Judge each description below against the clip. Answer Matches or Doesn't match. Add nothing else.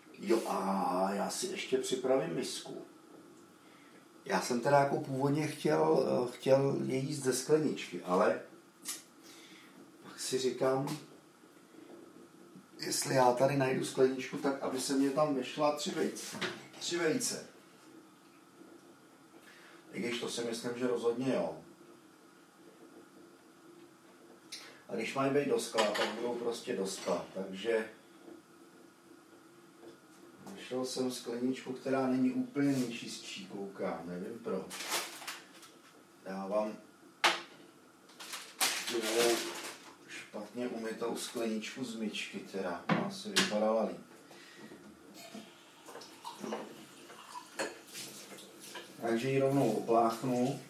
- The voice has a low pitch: Matches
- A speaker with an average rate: Doesn't match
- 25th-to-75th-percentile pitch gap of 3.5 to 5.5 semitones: Doesn't match